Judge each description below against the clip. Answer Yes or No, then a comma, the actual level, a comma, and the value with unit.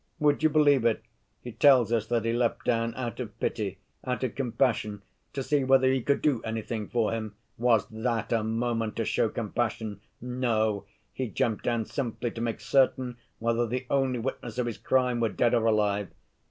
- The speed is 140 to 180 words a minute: No, average, 190 wpm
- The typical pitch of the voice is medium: No, low, 120 Hz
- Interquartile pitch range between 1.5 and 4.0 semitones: Yes, narrow, 2.4 semitones